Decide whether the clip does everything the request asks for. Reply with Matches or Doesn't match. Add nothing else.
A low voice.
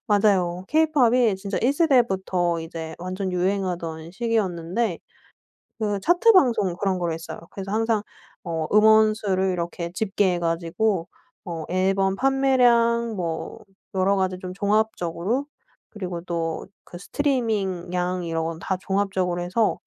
Doesn't match